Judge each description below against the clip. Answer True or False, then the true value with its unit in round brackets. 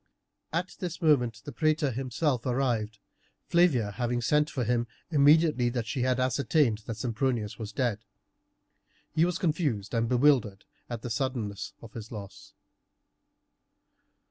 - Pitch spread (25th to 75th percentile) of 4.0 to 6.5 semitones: True (4.6 semitones)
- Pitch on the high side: False (125 Hz)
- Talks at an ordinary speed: False (130 wpm)